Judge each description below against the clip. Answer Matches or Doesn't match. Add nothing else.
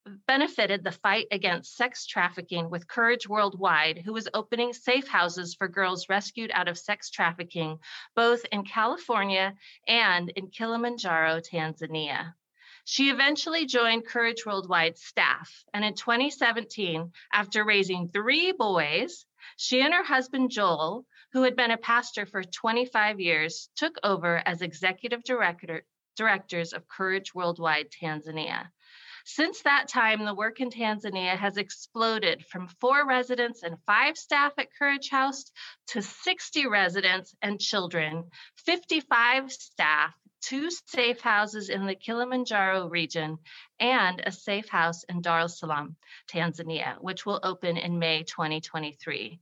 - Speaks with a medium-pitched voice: Doesn't match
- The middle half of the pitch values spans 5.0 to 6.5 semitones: Matches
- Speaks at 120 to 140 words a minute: Matches